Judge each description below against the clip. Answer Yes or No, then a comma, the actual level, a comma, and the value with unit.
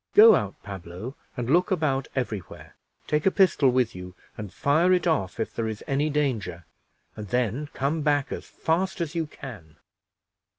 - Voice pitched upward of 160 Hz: No, low, 135 Hz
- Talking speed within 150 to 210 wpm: Yes, average, 175 wpm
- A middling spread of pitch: No, wide, 6.9 semitones